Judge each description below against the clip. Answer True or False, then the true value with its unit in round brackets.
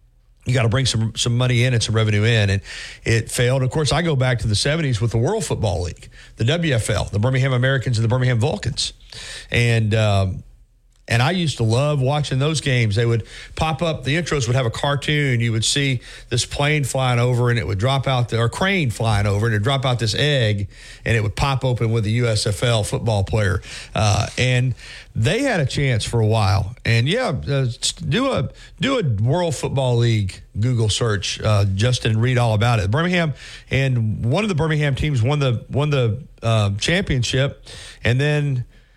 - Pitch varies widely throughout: False (3.5 semitones)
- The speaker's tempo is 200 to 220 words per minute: True (205 wpm)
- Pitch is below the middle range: True (120 Hz)